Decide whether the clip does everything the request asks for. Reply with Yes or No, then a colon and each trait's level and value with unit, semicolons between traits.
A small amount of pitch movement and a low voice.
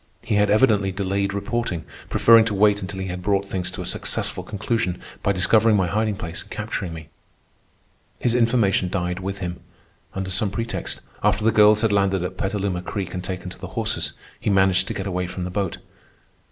Yes: narrow, 2.3 semitones; very low, 95 Hz